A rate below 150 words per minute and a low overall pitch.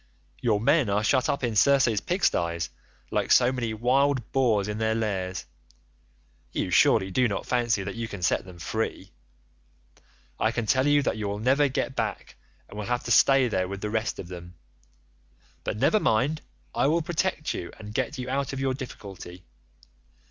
No: average, 185 wpm; low, 115 Hz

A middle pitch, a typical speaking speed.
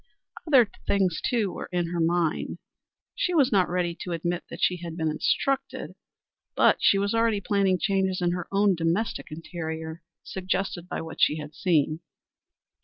Yes: medium, 180 Hz; average, 165 wpm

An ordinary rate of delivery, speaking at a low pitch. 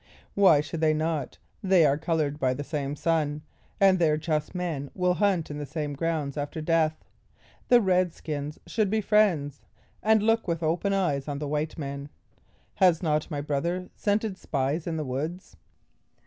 No: average, 175 wpm; medium, 160 Hz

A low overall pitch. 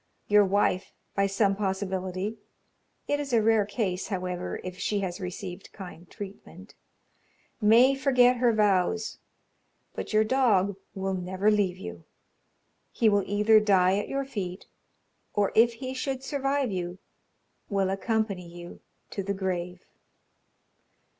No: high, 200 Hz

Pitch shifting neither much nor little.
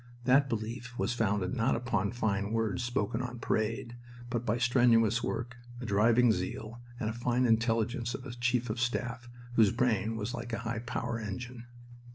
No: narrow, 1.8 semitones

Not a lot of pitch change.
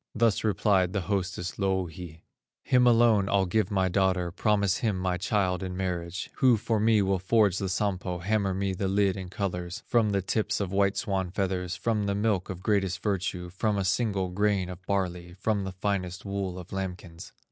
Yes: narrow, 2.0 semitones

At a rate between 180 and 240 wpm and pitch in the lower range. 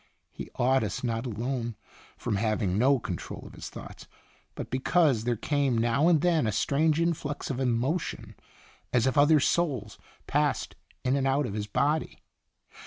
No: average, 170 wpm; low, 130 Hz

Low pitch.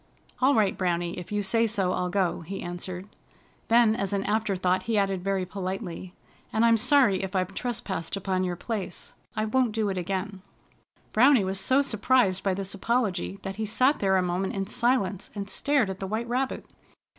No: high, 195 Hz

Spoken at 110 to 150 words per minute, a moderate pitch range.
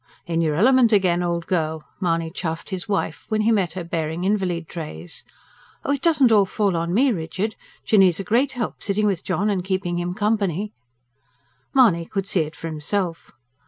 No: average, 185 wpm; average, 4.1 semitones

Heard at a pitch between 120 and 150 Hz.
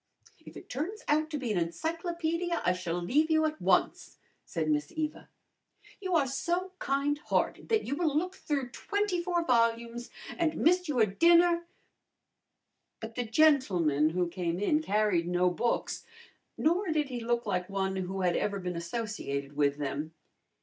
No: high, 245 Hz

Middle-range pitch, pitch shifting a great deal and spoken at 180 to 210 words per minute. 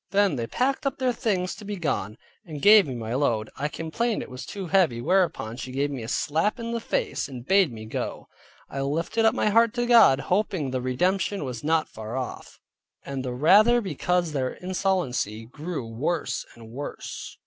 Yes: medium, 160 Hz; wide, 7.9 semitones; average, 195 wpm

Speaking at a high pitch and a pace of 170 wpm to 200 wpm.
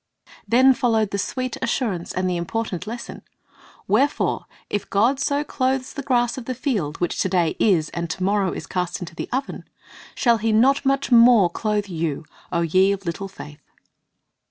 Yes: high, 210 Hz; average, 180 wpm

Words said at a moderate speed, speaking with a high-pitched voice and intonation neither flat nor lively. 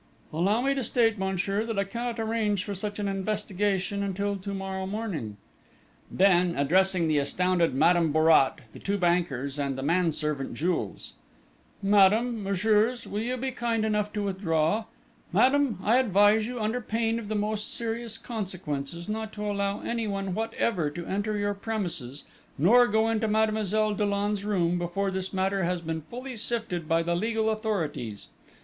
Yes: average, 160 wpm; high, 200 Hz; average, 3.8 semitones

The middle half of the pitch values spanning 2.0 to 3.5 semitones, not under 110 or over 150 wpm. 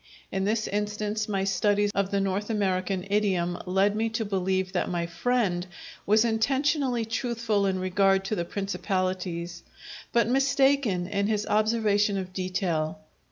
Yes: average, 2.8 semitones; average, 145 wpm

